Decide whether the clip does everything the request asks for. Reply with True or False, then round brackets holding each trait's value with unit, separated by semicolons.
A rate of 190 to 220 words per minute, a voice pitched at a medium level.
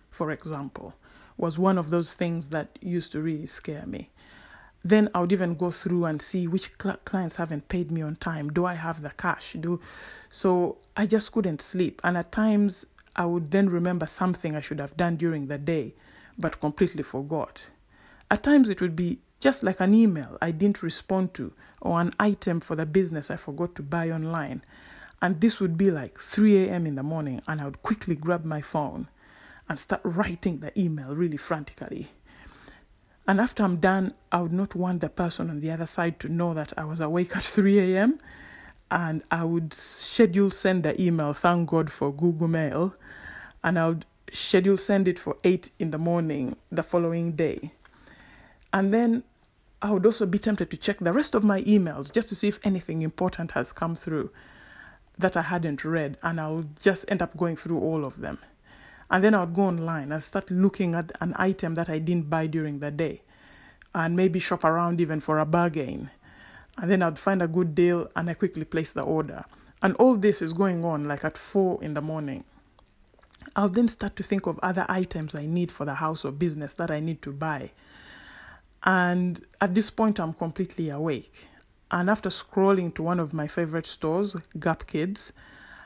True (195 wpm; 175 Hz)